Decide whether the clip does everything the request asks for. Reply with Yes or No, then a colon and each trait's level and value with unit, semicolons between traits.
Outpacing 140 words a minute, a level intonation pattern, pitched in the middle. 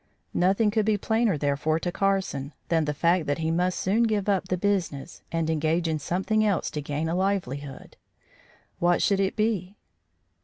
No: average, 180 wpm; average, 4.1 semitones; medium, 180 Hz